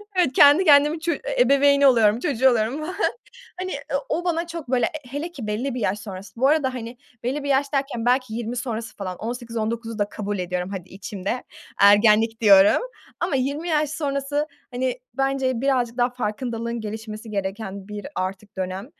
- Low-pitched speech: No, high, 245 Hz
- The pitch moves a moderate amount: Yes, average, 4.8 semitones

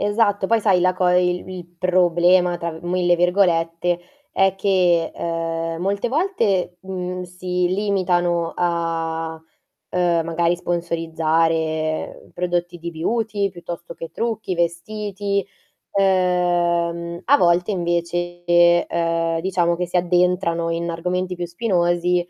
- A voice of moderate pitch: Yes, medium, 175 Hz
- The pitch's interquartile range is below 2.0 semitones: Yes, narrow, 1.5 semitones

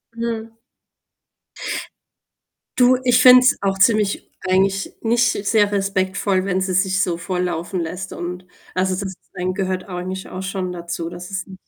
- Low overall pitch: No, high, 190 Hz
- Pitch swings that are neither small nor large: No, narrow, 1.9 semitones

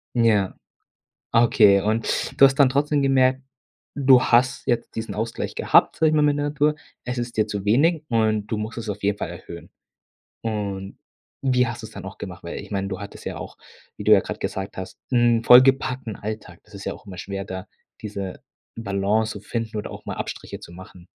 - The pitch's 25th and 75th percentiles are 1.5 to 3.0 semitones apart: No, average, 4.3 semitones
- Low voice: Yes, low, 110 Hz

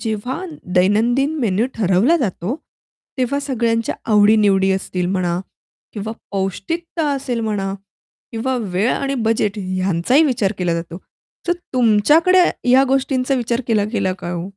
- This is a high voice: Yes, high, 220 Hz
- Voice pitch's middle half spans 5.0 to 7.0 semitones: Yes, average, 5.3 semitones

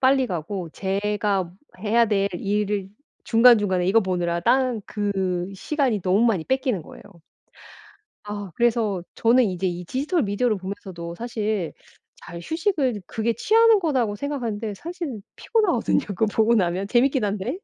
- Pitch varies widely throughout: No, average, 4.7 semitones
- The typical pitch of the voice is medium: No, high, 210 Hz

